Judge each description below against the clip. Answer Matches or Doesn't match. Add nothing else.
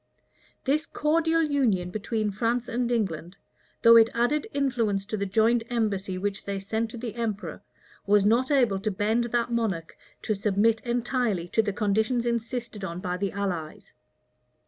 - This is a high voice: Matches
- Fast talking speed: Doesn't match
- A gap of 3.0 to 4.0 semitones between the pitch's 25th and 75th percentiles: Matches